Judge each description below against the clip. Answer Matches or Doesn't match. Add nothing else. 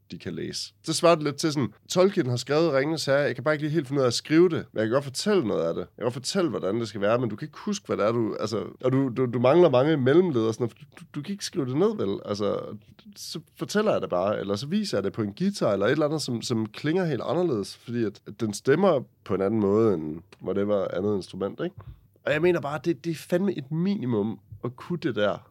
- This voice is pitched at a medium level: Matches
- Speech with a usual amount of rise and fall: Doesn't match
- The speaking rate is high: Matches